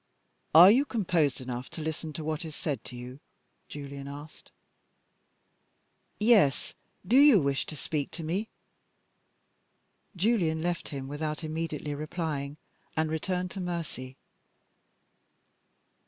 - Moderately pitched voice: Yes, medium, 155 Hz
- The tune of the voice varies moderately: Yes, average, 3.8 semitones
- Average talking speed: No, slow, 120 wpm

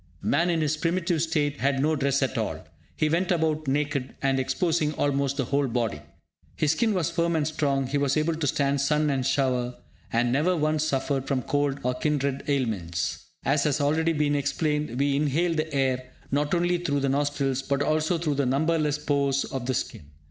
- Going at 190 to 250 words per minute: Yes, average, 195 wpm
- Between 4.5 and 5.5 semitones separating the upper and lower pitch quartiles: No, narrow, 2.5 semitones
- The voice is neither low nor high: Yes, medium, 145 Hz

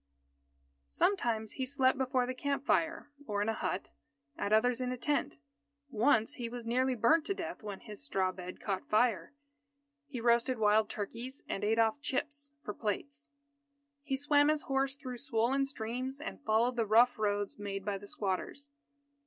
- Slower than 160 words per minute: No, average, 170 wpm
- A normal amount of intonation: Yes, average, 4.3 semitones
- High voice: Yes, high, 245 Hz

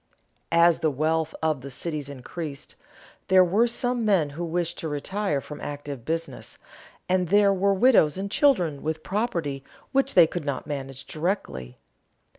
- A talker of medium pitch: Yes, medium, 165 Hz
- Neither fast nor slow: Yes, average, 155 wpm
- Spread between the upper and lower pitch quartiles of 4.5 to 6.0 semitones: Yes, average, 5.1 semitones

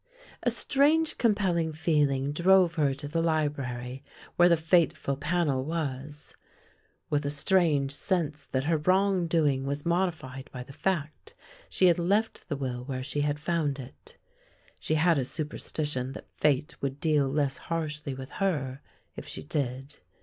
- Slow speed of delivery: No, average, 155 wpm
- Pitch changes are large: No, average, 3.7 semitones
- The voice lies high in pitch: No, medium, 150 Hz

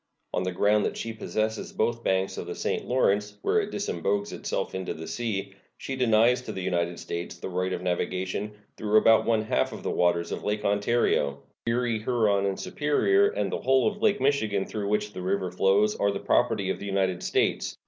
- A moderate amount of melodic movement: Yes, average, 3.7 semitones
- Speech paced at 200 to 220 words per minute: Yes, fast, 205 wpm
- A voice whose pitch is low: Yes, low, 105 Hz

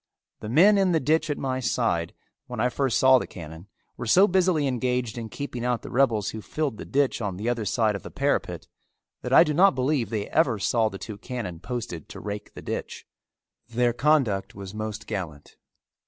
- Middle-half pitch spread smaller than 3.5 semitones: No, average, 4.6 semitones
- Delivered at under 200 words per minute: No, fast, 205 wpm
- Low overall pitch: Yes, low, 120 Hz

